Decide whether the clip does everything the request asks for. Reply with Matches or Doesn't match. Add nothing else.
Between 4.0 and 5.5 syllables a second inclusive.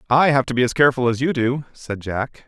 Doesn't match